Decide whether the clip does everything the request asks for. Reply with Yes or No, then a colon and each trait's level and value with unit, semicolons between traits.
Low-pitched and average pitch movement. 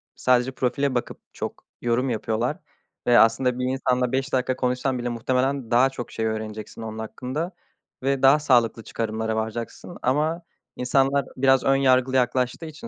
No: low, 125 Hz; narrow, 2.2 semitones